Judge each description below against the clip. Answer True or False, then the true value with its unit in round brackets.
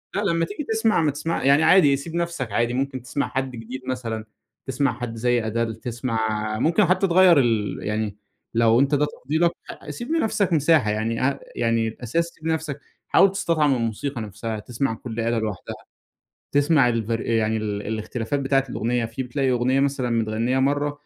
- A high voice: False (130 Hz)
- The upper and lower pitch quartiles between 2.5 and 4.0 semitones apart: False (4.8 semitones)